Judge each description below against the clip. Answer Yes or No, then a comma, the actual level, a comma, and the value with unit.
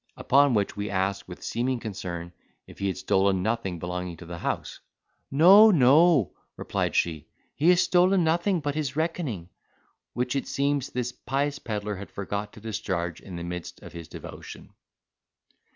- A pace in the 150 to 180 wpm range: Yes, average, 165 wpm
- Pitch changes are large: Yes, wide, 7.7 semitones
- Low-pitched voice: Yes, low, 110 Hz